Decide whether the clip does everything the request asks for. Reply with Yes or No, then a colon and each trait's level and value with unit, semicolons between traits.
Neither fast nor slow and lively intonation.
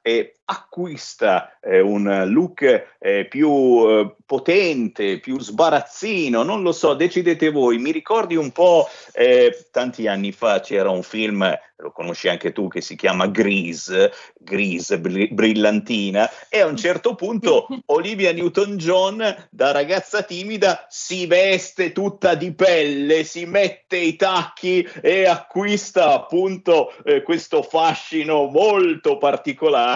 Yes: average, 130 wpm; wide, 8.1 semitones